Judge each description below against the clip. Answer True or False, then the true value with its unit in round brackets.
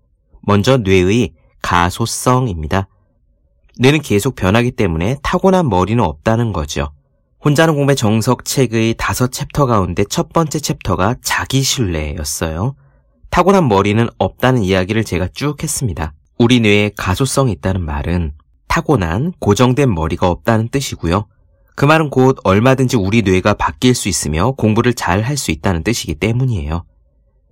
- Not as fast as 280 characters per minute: False (315 characters per minute)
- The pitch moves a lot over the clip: True (6.7 semitones)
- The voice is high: False (110 Hz)